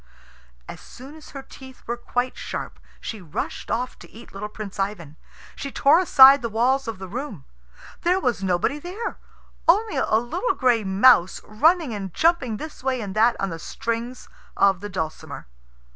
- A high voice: Yes, high, 240 Hz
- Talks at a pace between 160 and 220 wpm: Yes, average, 175 wpm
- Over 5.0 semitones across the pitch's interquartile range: Yes, wide, 5.5 semitones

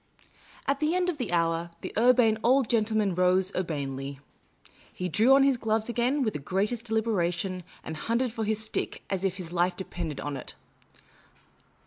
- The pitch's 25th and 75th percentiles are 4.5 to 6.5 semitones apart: Yes, average, 5.2 semitones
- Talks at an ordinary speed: Yes, average, 170 wpm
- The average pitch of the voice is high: Yes, high, 210 Hz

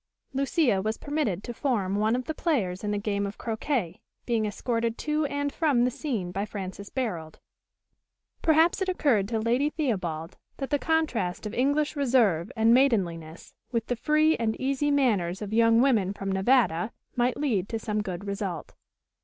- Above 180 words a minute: No, average, 170 wpm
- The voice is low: No, high, 230 Hz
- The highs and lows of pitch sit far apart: Yes, wide, 5.7 semitones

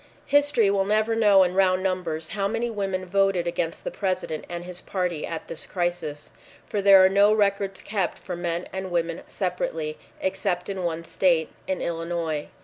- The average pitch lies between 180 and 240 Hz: Yes, medium, 185 Hz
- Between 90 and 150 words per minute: No, average, 175 wpm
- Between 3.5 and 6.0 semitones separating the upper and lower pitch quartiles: No, narrow, 2.4 semitones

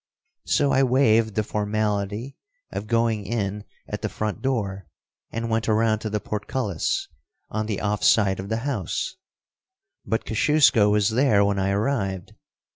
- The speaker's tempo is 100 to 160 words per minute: Yes, average, 150 wpm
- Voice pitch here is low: Yes, low, 110 Hz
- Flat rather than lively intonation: Yes, narrow, 2.3 semitones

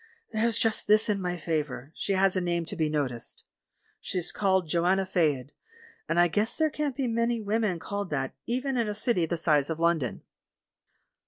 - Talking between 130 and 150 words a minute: No, average, 185 wpm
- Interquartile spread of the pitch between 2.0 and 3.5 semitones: No, average, 5.1 semitones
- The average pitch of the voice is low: No, medium, 185 Hz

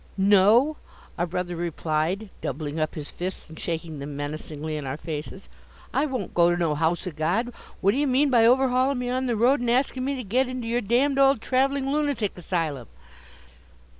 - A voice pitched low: No, high, 200 Hz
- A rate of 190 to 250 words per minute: Yes, average, 195 wpm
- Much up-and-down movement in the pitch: Yes, wide, 8.0 semitones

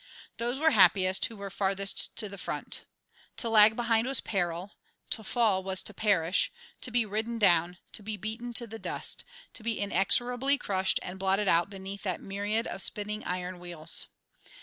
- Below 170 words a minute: No, average, 175 wpm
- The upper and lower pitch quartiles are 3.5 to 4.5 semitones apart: No, average, 2.9 semitones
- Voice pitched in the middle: No, high, 205 Hz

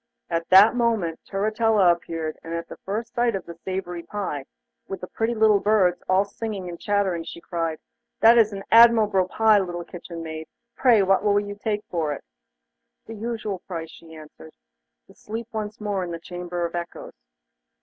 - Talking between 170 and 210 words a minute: Yes, average, 180 wpm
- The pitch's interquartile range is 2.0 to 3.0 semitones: No, average, 4.0 semitones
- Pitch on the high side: Yes, high, 195 Hz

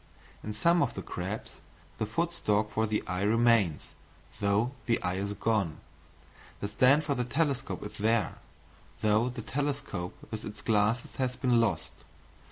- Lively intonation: No, average, 3.5 semitones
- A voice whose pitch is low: Yes, low, 110 Hz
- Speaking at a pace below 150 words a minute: No, average, 160 wpm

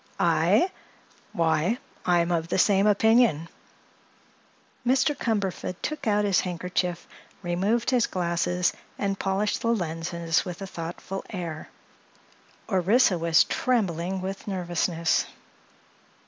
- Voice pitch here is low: No, medium, 185 Hz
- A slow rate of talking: Yes, slow, 105 wpm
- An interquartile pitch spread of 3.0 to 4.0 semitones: Yes, average, 3.5 semitones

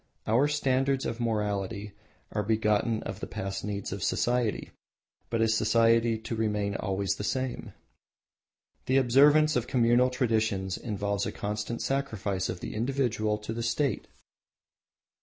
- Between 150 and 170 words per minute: No, average, 140 wpm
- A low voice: Yes, low, 110 Hz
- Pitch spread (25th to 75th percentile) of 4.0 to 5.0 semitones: No, average, 3.2 semitones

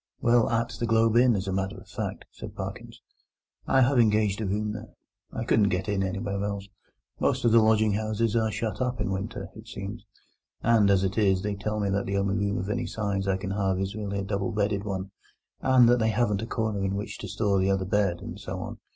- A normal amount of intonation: No, narrow, 2.3 semitones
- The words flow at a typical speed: No, fast, 235 wpm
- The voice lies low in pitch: Yes, low, 105 Hz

